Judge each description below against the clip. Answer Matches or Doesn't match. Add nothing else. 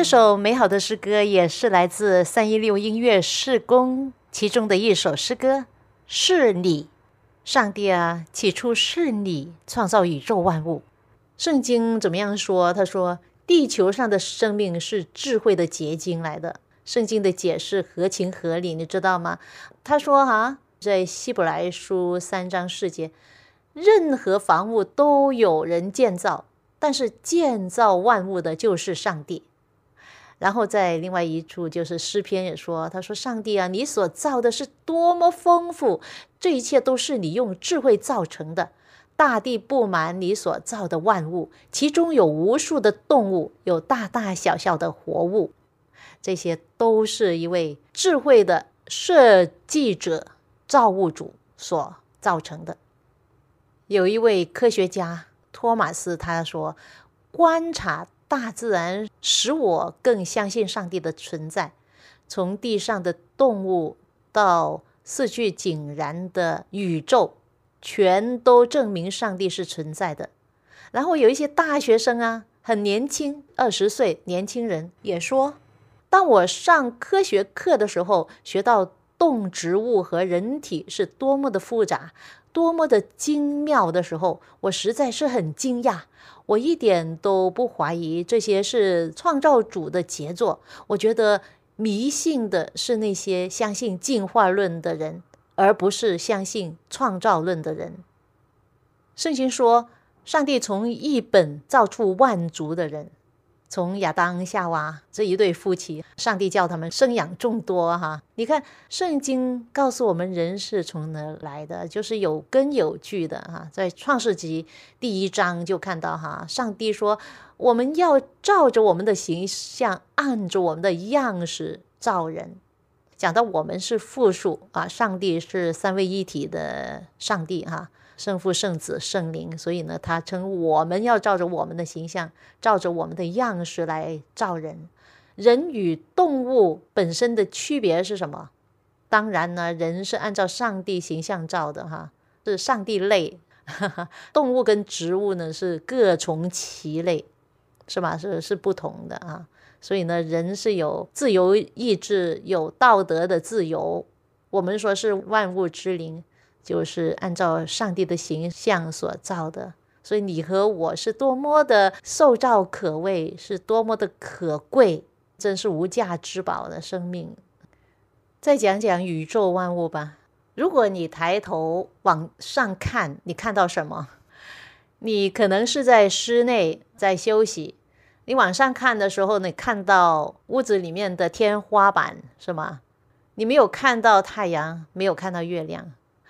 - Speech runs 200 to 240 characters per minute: Matches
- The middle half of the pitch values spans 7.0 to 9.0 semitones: Doesn't match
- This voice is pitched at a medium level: Doesn't match